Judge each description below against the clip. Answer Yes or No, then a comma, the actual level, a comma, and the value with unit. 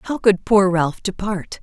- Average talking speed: Yes, average, 185 wpm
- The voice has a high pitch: Yes, high, 195 Hz